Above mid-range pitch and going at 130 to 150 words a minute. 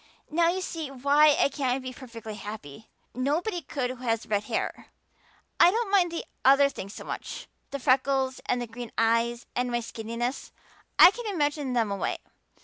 No: very high, 260 Hz; average, 175 wpm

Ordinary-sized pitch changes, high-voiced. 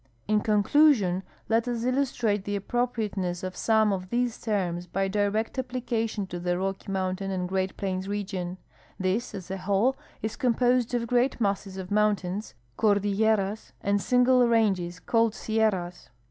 Yes: average, 3.3 semitones; high, 205 Hz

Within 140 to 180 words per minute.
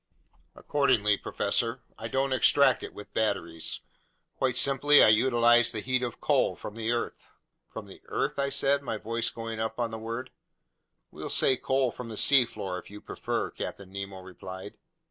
Yes: average, 170 wpm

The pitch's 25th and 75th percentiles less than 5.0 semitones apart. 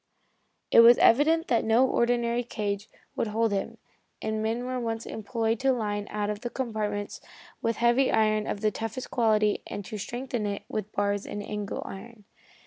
Yes: narrow, 2.4 semitones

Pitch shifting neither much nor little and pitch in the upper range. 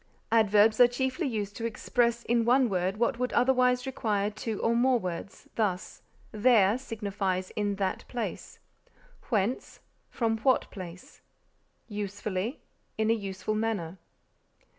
Yes: average, 3.3 semitones; high, 220 Hz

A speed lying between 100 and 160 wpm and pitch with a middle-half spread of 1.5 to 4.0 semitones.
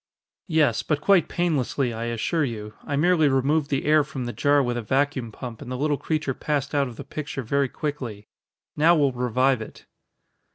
No: average, 195 wpm; average, 3.6 semitones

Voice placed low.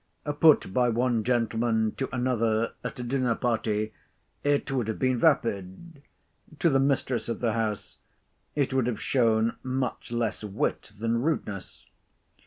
Yes: low, 120 Hz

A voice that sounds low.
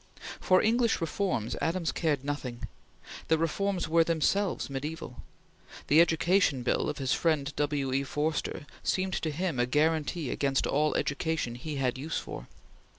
No: medium, 155 Hz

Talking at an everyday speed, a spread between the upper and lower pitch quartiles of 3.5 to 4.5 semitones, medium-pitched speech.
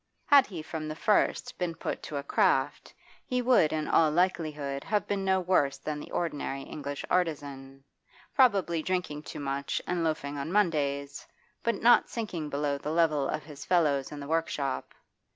Yes: average, 170 wpm; average, 4.2 semitones; medium, 155 Hz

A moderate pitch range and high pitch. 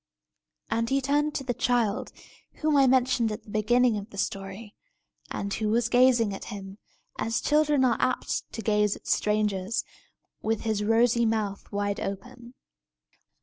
Yes: average, 3.3 semitones; high, 225 Hz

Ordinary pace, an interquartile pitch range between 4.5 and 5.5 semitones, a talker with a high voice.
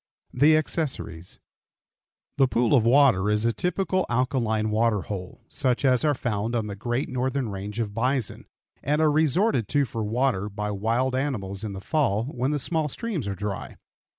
No: average, 175 wpm; average, 5.0 semitones; low, 120 Hz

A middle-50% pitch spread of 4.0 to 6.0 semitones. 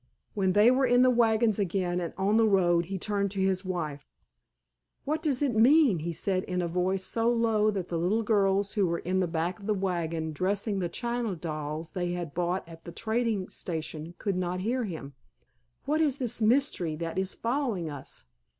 Yes: average, 4.6 semitones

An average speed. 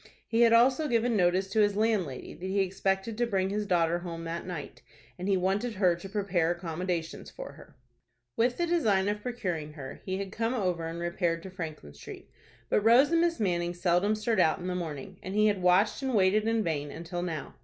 No: fast, 215 wpm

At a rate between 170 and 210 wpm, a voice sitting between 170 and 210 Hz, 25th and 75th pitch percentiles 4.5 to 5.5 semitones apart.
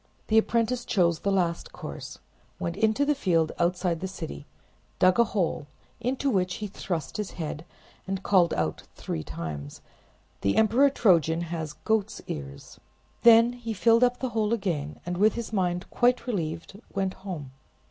No: average, 160 wpm; high, 190 Hz; average, 5.2 semitones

